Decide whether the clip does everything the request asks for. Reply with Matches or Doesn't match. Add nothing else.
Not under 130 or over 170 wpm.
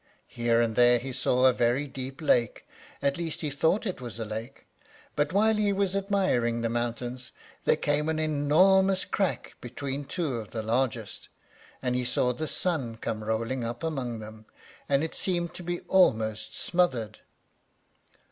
Matches